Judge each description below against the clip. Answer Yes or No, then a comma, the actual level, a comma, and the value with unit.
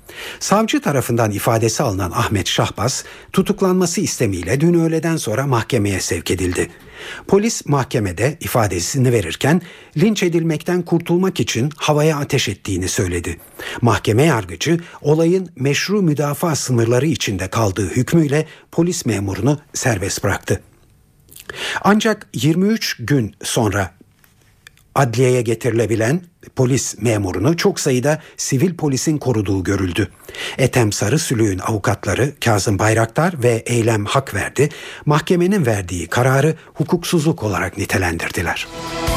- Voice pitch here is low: Yes, low, 130 Hz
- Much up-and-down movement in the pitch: Yes, wide, 6.6 semitones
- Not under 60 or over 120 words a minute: Yes, average, 105 wpm